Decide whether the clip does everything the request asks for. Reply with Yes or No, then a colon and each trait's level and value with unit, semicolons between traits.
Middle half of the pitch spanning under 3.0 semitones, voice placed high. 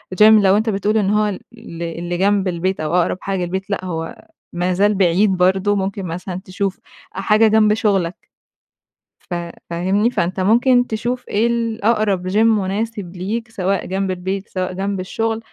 Yes: narrow, 2.6 semitones; high, 195 Hz